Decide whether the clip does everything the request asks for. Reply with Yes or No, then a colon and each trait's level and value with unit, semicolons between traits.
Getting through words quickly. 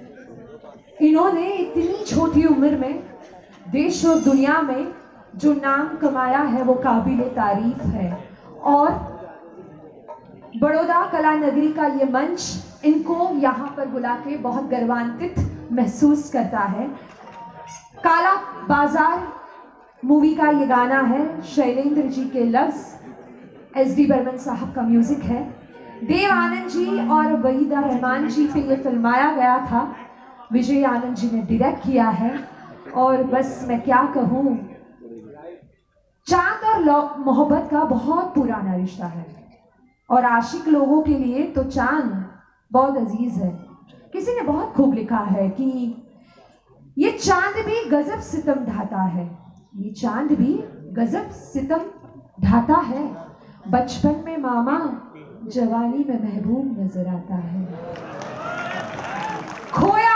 No: average, 125 wpm